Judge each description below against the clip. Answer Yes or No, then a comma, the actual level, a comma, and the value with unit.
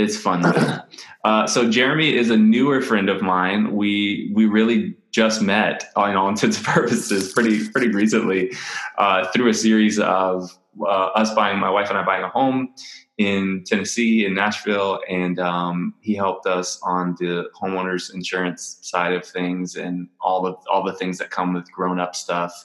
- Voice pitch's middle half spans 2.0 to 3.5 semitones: Yes, average, 3.2 semitones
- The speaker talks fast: No, average, 185 wpm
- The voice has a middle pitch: No, very low, 95 Hz